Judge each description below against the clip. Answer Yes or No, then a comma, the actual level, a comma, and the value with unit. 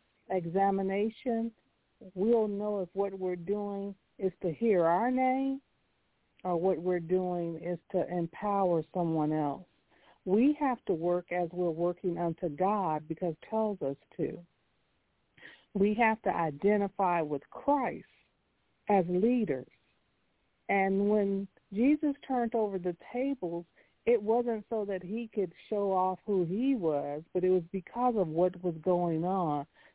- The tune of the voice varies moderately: Yes, average, 3.6 semitones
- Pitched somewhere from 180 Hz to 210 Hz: Yes, high, 190 Hz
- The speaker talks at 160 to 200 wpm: No, average, 140 wpm